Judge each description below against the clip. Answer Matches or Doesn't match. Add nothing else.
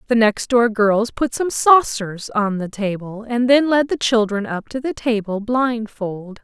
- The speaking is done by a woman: Matches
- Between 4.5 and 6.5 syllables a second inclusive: Doesn't match